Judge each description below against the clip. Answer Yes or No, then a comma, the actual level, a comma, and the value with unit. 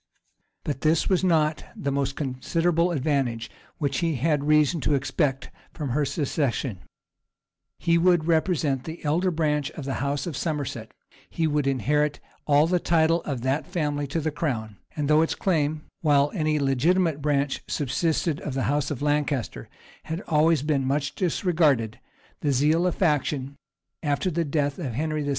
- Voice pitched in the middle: Yes, medium, 150 Hz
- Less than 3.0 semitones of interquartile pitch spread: Yes, narrow, 2.6 semitones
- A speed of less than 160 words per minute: No, average, 165 wpm